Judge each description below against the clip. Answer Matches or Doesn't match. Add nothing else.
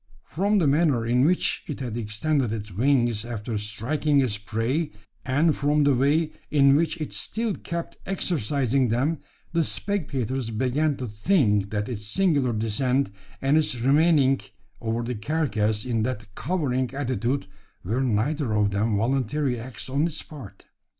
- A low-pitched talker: Matches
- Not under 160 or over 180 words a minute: Doesn't match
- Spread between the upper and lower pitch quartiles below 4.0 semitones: Doesn't match